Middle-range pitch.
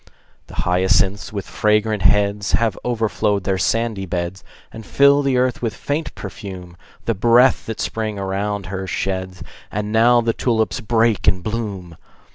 No: low, 105 Hz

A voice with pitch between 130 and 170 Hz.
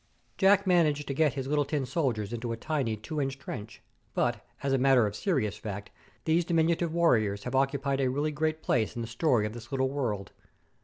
Yes: low, 135 Hz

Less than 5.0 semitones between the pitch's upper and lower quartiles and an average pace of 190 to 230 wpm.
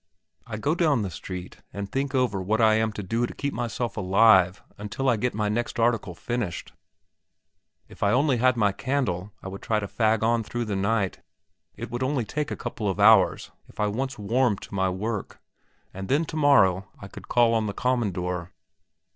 Yes: average, 3.7 semitones; average, 195 wpm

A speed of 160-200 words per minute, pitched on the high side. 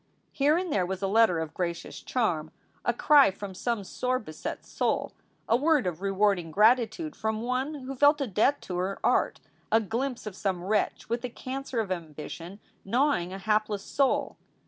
Yes: average, 180 wpm; high, 215 Hz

